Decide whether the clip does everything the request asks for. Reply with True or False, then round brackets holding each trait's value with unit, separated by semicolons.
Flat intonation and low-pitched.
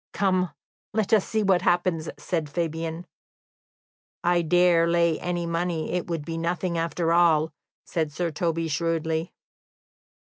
False (1.4 semitones; 170 Hz)